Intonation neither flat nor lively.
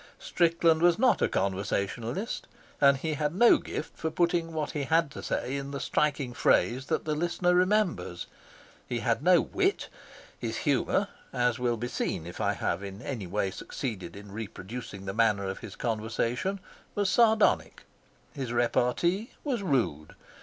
No: wide, 7.5 semitones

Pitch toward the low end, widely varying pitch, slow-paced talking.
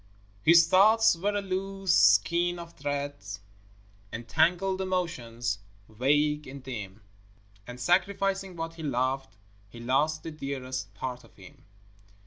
No: medium, 150 Hz; wide, 6.2 semitones; slow, 125 wpm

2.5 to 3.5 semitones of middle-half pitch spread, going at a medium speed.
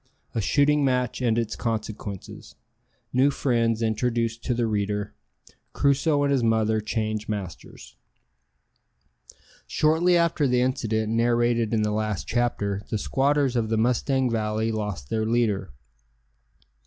No: average, 2.8 semitones; slow, 130 wpm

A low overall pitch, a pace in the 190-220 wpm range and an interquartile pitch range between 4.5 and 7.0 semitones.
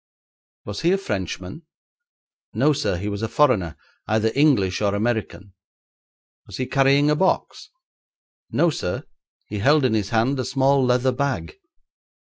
No: low, 125 Hz; average, 145 wpm; wide, 5.5 semitones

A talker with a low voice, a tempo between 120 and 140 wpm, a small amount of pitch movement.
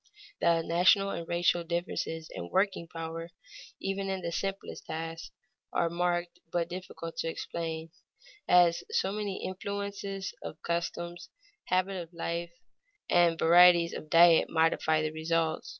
No: medium, 170 Hz; slow, 135 wpm; narrow, 2.0 semitones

